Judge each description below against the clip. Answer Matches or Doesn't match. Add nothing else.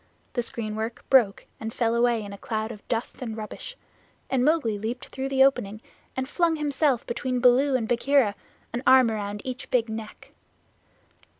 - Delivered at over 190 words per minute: Doesn't match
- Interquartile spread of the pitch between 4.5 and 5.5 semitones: Doesn't match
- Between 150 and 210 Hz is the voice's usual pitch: Doesn't match